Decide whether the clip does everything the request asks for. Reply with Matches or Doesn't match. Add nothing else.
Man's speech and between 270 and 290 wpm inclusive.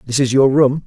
Matches